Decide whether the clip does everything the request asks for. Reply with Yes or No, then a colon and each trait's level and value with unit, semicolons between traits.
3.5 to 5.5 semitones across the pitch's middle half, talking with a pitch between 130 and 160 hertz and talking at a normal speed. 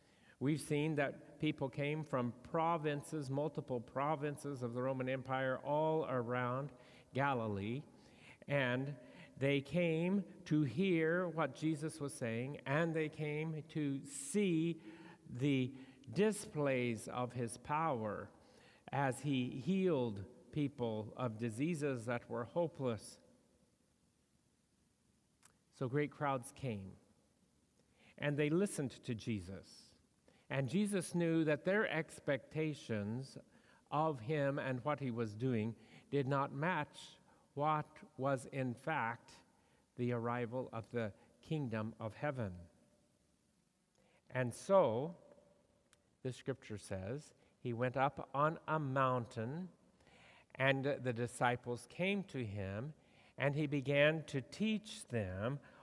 No: average, 4.0 semitones; medium, 140 Hz; slow, 110 wpm